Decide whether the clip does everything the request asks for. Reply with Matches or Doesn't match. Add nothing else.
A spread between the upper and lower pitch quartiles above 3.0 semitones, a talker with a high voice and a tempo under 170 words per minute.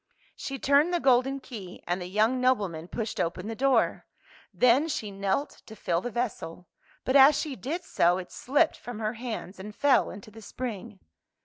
Doesn't match